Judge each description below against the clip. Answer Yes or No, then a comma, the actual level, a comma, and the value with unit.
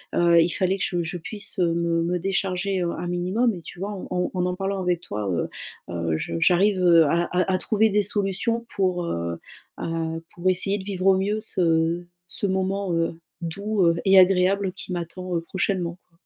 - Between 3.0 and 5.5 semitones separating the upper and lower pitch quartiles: No, narrow, 2.4 semitones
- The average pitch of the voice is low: No, medium, 180 Hz